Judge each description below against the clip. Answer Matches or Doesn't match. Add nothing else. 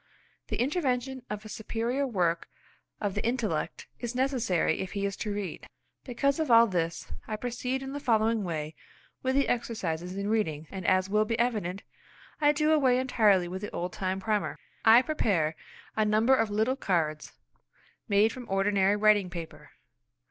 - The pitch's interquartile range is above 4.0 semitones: Matches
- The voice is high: Matches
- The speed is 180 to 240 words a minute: Doesn't match